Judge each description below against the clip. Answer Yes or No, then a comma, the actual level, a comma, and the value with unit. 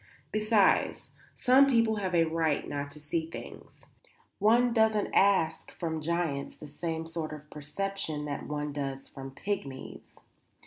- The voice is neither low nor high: Yes, medium, 165 Hz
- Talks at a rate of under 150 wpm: Yes, average, 140 wpm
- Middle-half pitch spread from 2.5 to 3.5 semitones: No, average, 5.3 semitones